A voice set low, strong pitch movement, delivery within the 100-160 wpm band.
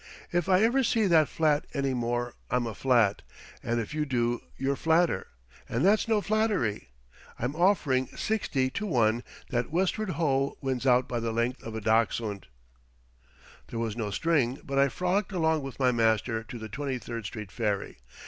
No: low, 130 Hz; wide, 5.7 semitones; average, 175 wpm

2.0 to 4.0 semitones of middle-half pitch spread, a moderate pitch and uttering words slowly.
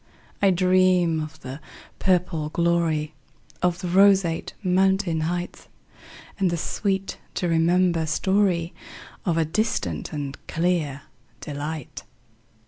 Yes: average, 2.8 semitones; medium, 170 Hz; slow, 95 wpm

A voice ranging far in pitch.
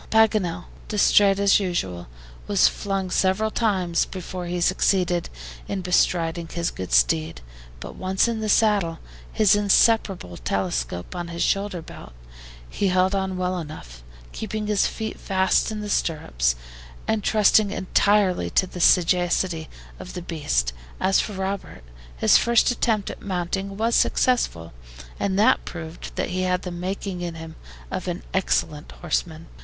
No: average, 3.2 semitones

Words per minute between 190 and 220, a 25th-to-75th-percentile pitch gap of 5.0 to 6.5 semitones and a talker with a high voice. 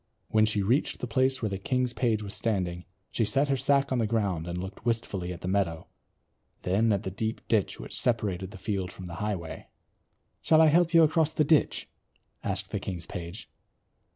No: average, 200 wpm; wide, 5.5 semitones; low, 105 Hz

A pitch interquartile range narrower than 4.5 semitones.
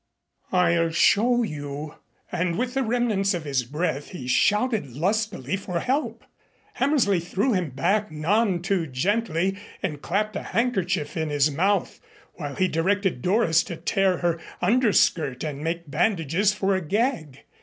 No: average, 5.0 semitones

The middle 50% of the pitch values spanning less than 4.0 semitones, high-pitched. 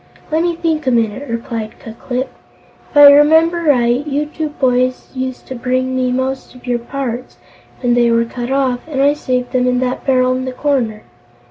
Yes: narrow, 2.5 semitones; very high, 255 Hz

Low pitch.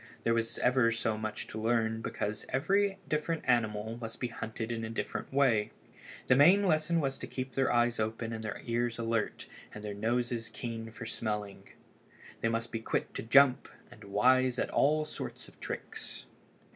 Yes: low, 115 Hz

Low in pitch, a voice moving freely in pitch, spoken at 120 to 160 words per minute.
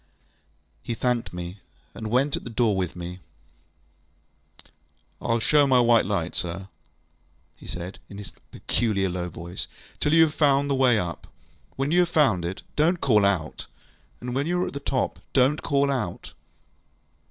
No: low, 120 Hz; wide, 7.0 semitones; average, 175 wpm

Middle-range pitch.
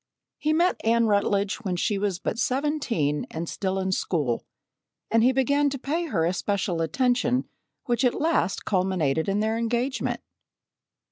No: high, 215 Hz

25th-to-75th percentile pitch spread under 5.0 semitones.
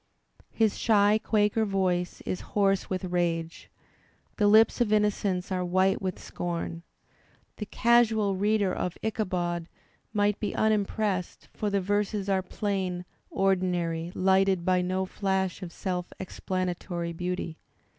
Yes: narrow, 2.4 semitones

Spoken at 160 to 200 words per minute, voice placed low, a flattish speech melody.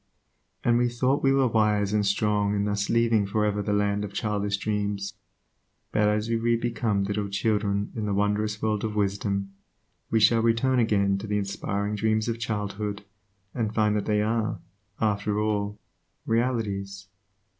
Yes: average, 165 wpm; low, 105 Hz; narrow, 1.7 semitones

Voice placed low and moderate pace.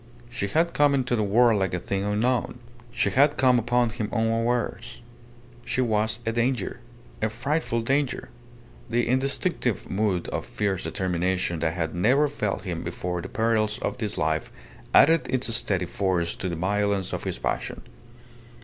Yes: low, 110 Hz; average, 160 wpm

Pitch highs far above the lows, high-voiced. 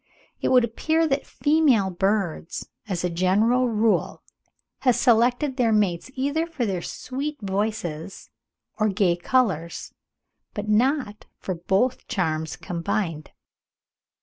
Yes: wide, 5.8 semitones; high, 215 Hz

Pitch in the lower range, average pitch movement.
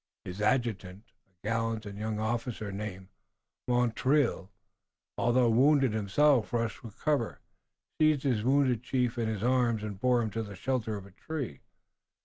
Yes: low, 115 Hz; average, 3.3 semitones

